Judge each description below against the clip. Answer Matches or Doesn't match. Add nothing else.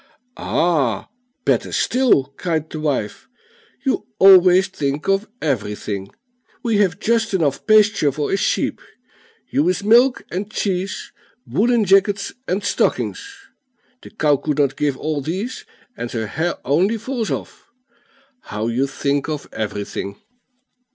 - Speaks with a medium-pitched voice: Matches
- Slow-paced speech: Matches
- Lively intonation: Matches